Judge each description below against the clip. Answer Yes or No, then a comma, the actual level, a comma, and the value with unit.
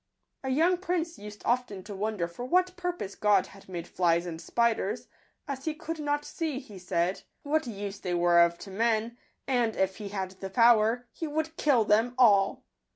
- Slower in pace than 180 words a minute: No, average, 190 wpm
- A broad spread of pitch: Yes, wide, 6.9 semitones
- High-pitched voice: Yes, high, 220 Hz